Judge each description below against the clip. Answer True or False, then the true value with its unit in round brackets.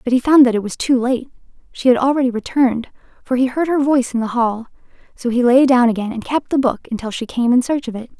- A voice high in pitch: True (250 Hz)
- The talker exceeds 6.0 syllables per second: True (6.3 syllables/s)